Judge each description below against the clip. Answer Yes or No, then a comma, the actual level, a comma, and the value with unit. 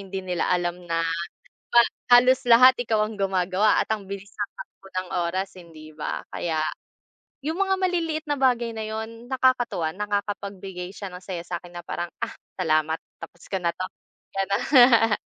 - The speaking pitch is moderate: No, high, 200 Hz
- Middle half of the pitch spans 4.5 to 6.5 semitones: Yes, average, 5.0 semitones